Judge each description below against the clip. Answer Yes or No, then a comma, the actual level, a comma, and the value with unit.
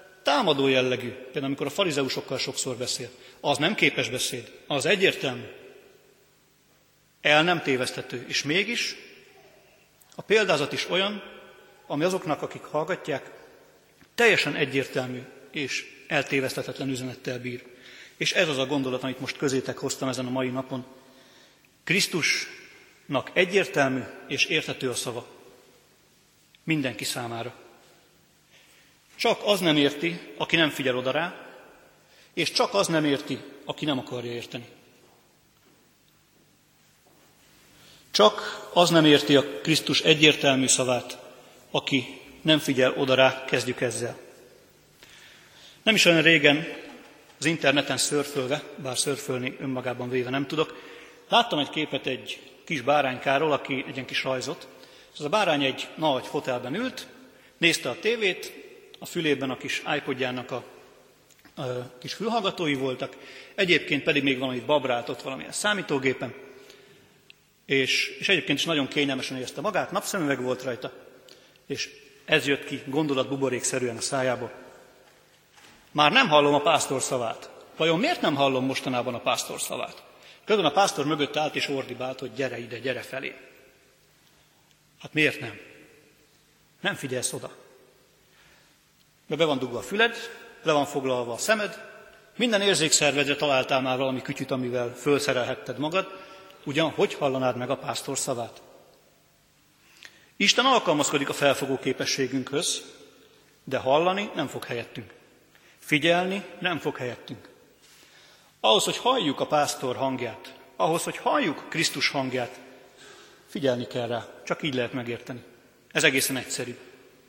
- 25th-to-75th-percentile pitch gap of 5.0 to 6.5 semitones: No, average, 3.6 semitones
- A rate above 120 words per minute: Yes, average, 130 wpm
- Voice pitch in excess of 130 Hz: Yes, medium, 140 Hz